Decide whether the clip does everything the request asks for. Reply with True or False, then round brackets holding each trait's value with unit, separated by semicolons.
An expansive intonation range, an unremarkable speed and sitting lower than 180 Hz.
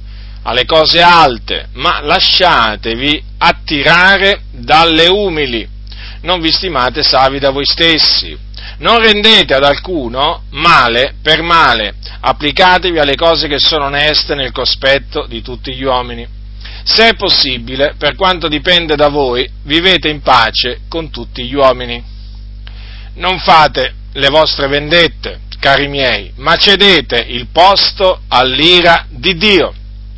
True (6.3 semitones; 125 wpm; 140 Hz)